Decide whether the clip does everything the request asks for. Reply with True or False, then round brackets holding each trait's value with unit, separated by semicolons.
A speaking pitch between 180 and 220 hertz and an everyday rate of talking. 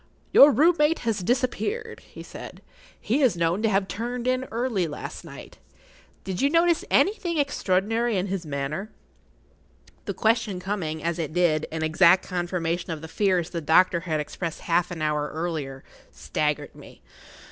True (185 Hz; 165 wpm)